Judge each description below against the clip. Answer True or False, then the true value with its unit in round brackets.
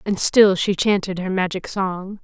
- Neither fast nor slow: True (190 wpm)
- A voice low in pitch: False (190 Hz)